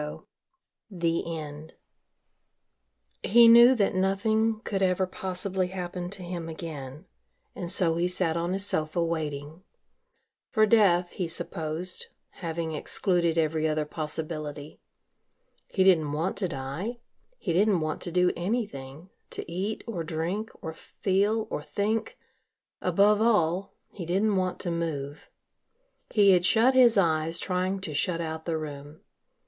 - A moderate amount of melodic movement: Yes, average, 3.6 semitones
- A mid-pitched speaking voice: Yes, medium, 175 Hz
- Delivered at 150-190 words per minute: No, average, 140 wpm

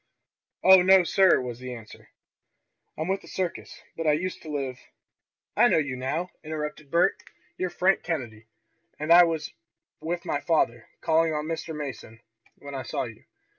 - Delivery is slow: No, average, 170 wpm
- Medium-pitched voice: Yes, medium, 155 Hz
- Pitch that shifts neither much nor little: Yes, average, 4.7 semitones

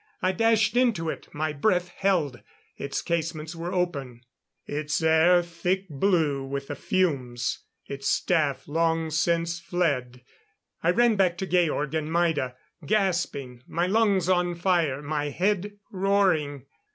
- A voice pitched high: No, medium, 165 Hz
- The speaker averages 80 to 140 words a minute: Yes, slow, 135 wpm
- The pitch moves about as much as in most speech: Yes, average, 4.1 semitones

